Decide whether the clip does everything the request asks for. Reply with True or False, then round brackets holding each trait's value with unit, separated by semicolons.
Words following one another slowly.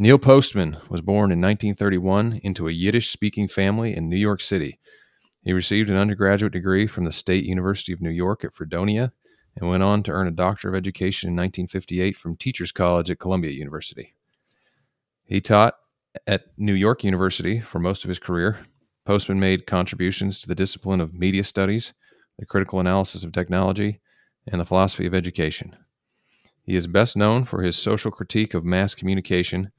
False (175 wpm)